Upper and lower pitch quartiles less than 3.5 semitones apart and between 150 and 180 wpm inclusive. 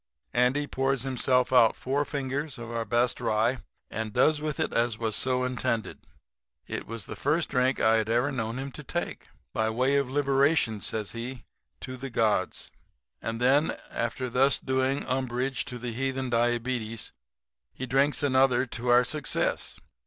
Yes: narrow, 2.5 semitones; average, 165 wpm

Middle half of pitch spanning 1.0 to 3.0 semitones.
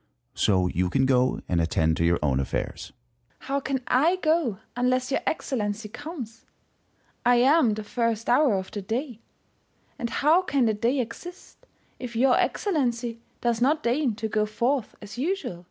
No: average, 4.8 semitones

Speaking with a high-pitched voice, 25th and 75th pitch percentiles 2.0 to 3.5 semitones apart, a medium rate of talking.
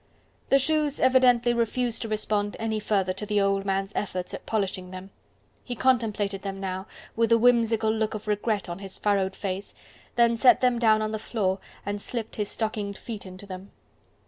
Yes: high, 215 Hz; average, 2.9 semitones; average, 185 wpm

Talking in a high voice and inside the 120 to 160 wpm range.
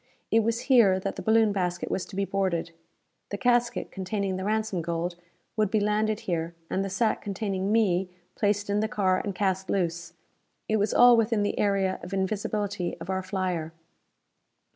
No: high, 195 Hz; average, 180 wpm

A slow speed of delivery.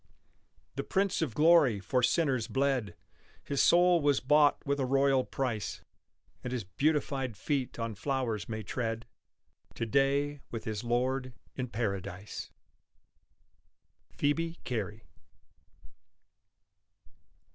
Yes: slow, 110 wpm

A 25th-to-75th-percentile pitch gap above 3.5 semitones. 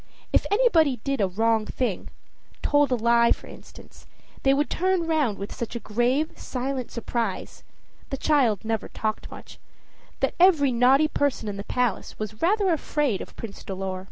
Yes: average, 5.1 semitones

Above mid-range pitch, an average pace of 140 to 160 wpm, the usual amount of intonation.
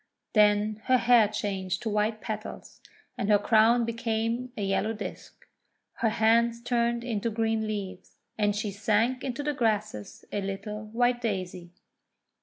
No: high, 220 Hz; average, 145 wpm; narrow, 2.1 semitones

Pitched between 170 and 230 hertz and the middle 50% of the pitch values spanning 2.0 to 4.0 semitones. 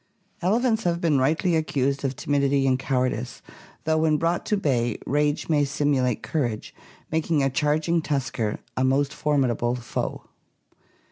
No: medium, 145 Hz; average, 3.4 semitones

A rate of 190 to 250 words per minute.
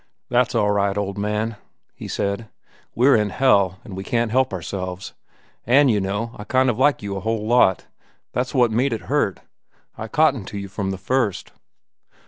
No: average, 180 wpm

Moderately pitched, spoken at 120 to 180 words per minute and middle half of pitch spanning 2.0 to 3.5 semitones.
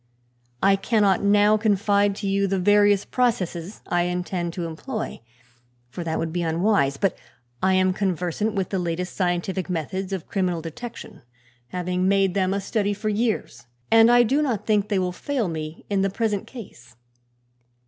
No: high, 195 Hz; average, 170 wpm; average, 2.8 semitones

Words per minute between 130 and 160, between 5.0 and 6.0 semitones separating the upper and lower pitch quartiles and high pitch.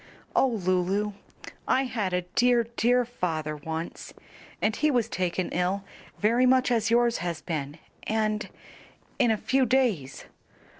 Yes: average, 140 wpm; wide, 5.4 semitones; high, 215 Hz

